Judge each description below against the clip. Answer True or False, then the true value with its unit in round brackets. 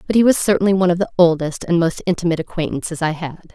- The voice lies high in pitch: False (170 Hz)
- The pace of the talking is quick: True (235 wpm)